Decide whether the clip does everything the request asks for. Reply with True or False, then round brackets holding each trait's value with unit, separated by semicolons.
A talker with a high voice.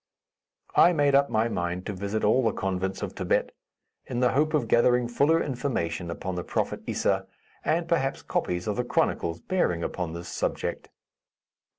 False (110 Hz)